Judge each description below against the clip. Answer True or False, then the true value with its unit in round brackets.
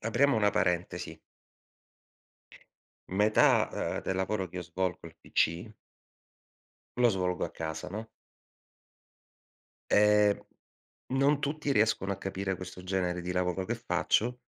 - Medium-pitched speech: False (95 Hz)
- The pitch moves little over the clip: False (3.2 semitones)